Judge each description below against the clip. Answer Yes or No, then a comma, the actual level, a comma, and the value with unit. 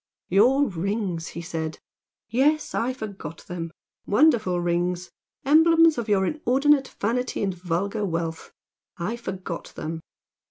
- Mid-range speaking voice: No, high, 200 Hz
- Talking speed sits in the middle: No, slow, 120 wpm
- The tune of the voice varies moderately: No, wide, 6.6 semitones